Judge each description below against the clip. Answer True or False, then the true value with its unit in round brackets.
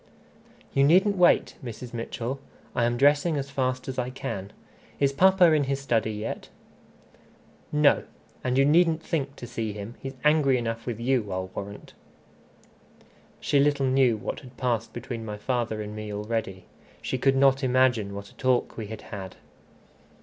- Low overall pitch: True (125 Hz)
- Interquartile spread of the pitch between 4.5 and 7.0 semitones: False (3.7 semitones)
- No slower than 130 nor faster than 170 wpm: True (165 wpm)